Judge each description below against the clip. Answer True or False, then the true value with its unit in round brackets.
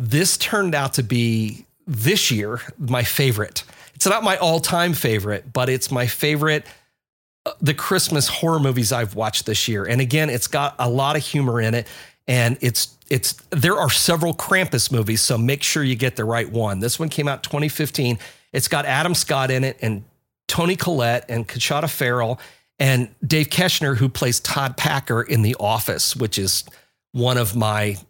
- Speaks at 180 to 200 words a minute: True (185 wpm)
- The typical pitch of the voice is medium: False (130 Hz)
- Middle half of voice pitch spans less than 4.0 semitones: False (4.4 semitones)